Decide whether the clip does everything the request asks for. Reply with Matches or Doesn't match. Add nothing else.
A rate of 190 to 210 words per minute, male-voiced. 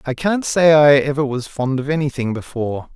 Matches